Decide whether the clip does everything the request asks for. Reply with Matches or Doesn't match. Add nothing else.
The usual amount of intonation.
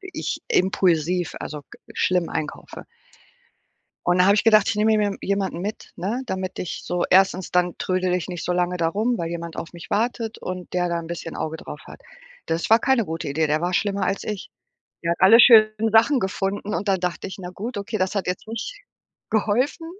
Matches